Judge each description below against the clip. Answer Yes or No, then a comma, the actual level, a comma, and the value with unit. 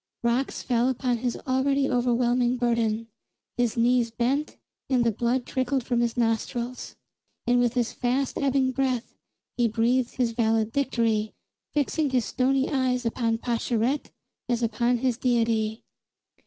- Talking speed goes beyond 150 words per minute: No, slow, 135 wpm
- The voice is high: Yes, high, 245 Hz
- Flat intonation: Yes, narrow, 1.8 semitones